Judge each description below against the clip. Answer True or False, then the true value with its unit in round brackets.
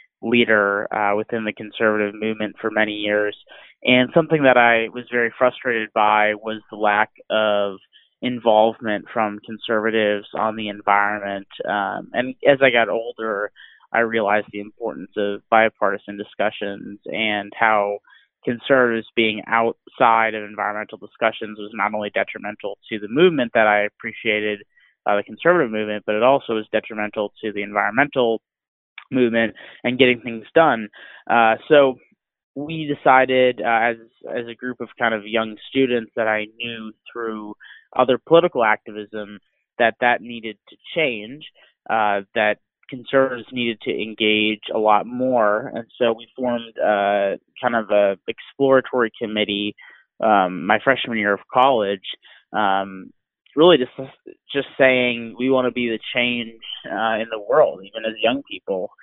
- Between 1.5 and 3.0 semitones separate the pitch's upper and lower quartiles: True (2.6 semitones)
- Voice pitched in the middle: False (110 Hz)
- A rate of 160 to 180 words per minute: False (145 wpm)